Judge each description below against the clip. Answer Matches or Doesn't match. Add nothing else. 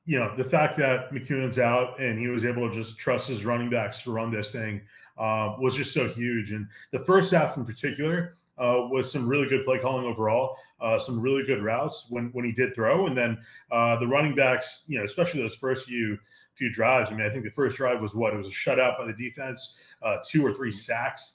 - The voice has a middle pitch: Doesn't match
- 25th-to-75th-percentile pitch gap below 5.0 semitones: Matches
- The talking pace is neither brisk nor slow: Doesn't match